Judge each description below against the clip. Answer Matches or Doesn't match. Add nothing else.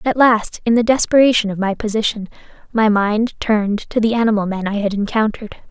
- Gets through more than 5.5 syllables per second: Matches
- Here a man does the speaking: Doesn't match